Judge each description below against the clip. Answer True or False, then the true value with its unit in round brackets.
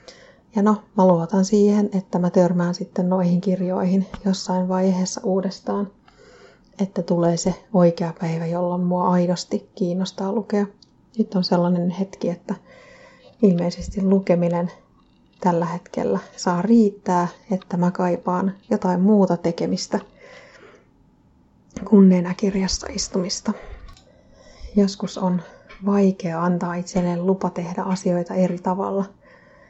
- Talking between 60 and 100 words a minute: False (110 wpm)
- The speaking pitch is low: False (185 Hz)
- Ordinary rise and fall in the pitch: False (1.8 semitones)